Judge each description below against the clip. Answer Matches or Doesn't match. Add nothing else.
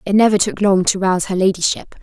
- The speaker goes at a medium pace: Doesn't match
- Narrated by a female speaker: Matches